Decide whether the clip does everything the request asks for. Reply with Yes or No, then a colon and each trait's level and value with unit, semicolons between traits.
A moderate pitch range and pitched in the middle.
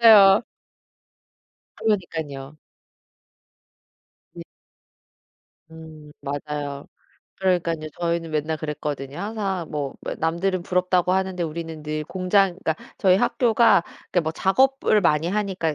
Yes: average, 3.9 semitones; medium, 170 Hz